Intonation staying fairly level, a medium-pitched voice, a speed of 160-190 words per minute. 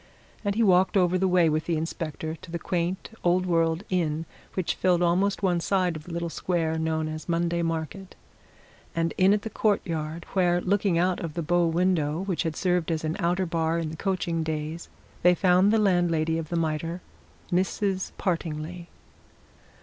Yes: narrow, 2.2 semitones; medium, 170 Hz; average, 180 wpm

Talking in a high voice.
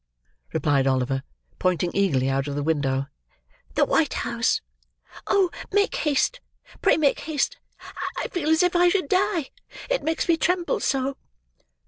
Yes: very high, 275 Hz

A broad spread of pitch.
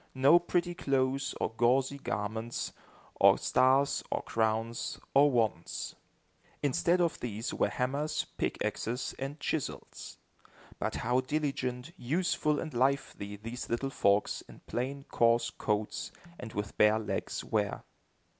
No: average, 3.6 semitones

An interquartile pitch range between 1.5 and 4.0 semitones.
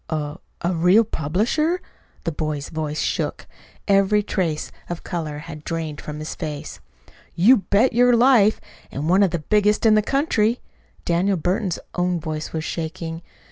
No: average, 5.0 semitones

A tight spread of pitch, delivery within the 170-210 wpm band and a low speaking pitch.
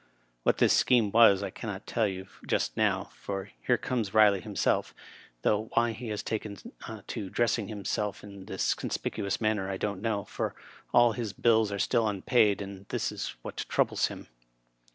Yes: narrow, 2.3 semitones; average, 180 wpm; low, 105 Hz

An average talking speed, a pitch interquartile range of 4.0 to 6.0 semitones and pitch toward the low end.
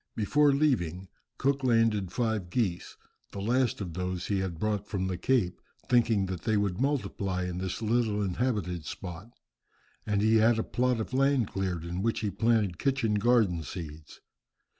Yes: average, 165 wpm; average, 4.5 semitones; low, 105 Hz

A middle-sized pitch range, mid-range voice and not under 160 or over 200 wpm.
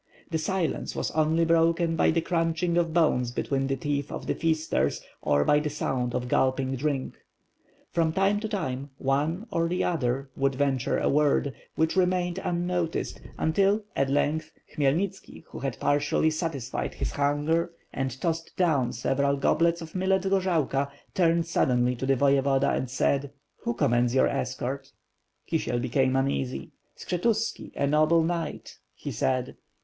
Yes: average, 3.8 semitones; medium, 150 Hz; average, 165 wpm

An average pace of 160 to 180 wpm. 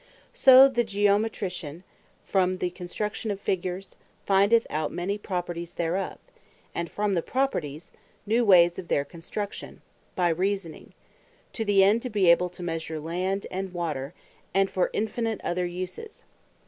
No: average, 145 wpm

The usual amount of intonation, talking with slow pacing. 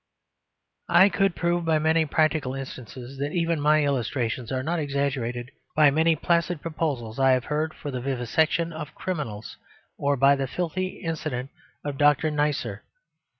No: average, 3.4 semitones; average, 150 wpm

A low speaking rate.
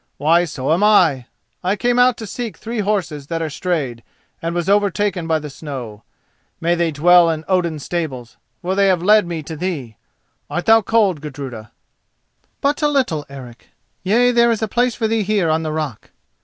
No: average, 185 wpm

